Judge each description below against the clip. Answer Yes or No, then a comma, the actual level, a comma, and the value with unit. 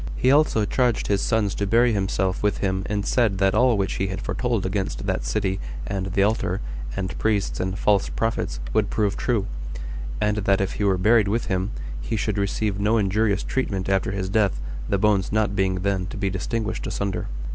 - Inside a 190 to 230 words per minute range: Yes, average, 200 wpm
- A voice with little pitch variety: Yes, narrow, 2.2 semitones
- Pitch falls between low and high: No, low, 100 Hz